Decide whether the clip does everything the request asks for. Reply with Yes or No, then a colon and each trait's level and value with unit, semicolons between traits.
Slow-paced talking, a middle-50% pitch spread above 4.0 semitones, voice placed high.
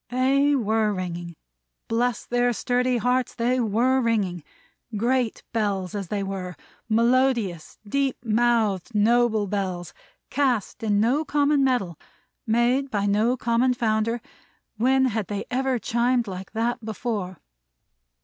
No: slow, 125 wpm; average, 3.5 semitones; high, 230 Hz